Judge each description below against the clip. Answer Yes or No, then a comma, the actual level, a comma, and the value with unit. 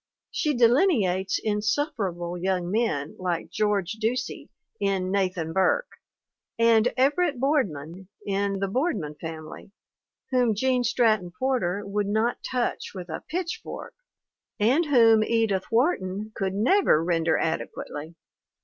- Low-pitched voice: No, high, 210 Hz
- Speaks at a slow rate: Yes, slow, 120 wpm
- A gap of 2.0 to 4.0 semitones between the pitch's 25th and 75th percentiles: No, average, 5.2 semitones